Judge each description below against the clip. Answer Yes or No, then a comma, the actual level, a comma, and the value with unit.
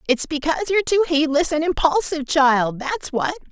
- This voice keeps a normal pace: Yes, average, 170 wpm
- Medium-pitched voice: No, very high, 290 Hz